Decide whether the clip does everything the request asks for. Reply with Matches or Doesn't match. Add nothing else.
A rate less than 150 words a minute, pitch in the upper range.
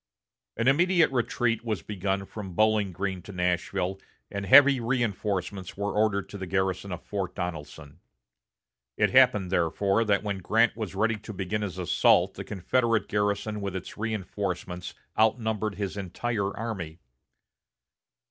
Doesn't match